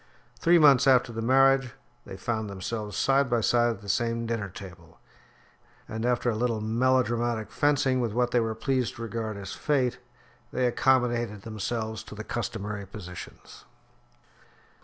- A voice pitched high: No, low, 115 Hz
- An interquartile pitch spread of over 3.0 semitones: No, narrow, 2.6 semitones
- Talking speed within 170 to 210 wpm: No, average, 155 wpm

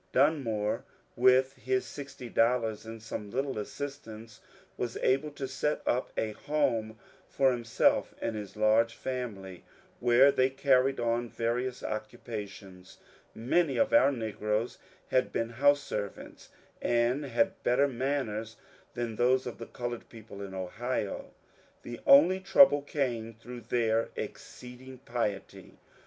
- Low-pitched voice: Yes, low, 120 Hz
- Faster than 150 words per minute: No, slow, 135 wpm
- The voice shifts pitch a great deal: No, average, 3.4 semitones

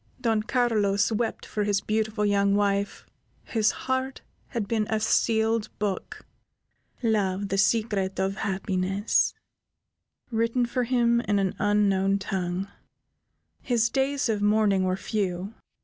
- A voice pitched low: No, high, 210 Hz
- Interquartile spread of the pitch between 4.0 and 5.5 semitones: No, narrow, 2.6 semitones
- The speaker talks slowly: Yes, slow, 125 wpm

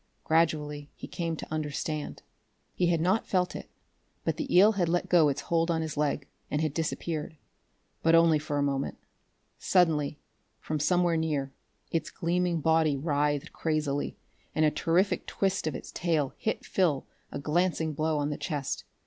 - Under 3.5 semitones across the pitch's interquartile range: Yes, narrow, 2.6 semitones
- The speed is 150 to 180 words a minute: Yes, average, 165 wpm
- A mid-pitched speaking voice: Yes, medium, 160 Hz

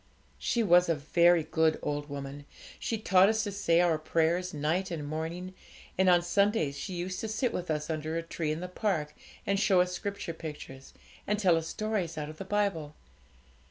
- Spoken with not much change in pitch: No, average, 3.7 semitones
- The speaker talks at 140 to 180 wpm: No, average, 195 wpm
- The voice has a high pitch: No, medium, 170 Hz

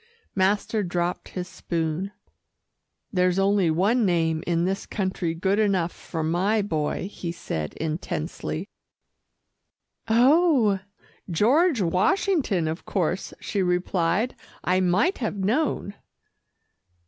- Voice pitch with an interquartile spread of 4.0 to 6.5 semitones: No, average, 3.5 semitones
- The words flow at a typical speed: No, slow, 105 wpm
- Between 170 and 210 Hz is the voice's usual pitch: Yes, medium, 185 Hz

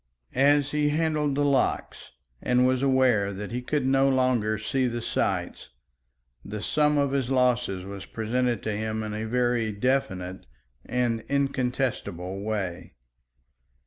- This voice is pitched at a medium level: No, low, 125 Hz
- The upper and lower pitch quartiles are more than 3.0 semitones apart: Yes, average, 4.0 semitones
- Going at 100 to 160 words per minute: Yes, average, 140 wpm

